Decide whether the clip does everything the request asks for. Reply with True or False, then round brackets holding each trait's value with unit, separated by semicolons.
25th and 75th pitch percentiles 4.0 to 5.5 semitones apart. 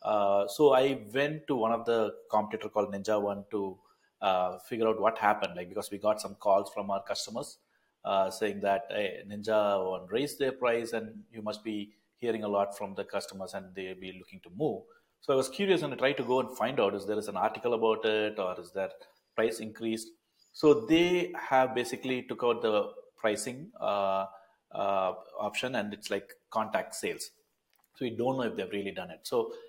True (4.5 semitones)